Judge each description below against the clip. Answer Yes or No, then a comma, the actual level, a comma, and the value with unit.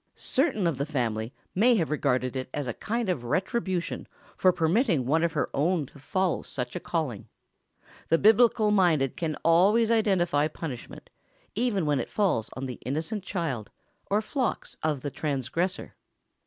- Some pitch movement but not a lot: No, wide, 6.4 semitones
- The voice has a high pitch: No, medium, 165 Hz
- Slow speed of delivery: No, average, 160 wpm